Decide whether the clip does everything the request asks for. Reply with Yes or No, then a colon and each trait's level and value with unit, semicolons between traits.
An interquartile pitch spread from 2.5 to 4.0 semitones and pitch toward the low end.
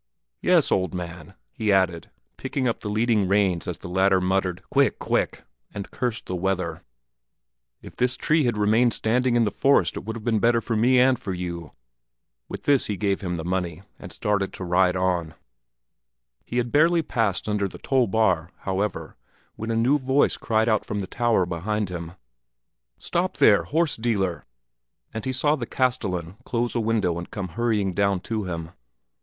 No: average, 4.4 semitones; low, 105 Hz